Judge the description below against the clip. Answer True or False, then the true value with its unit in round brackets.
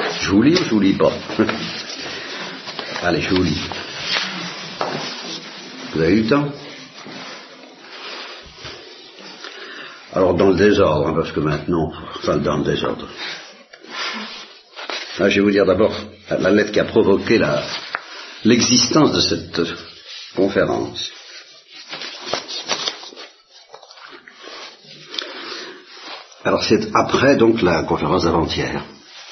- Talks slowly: True (105 wpm)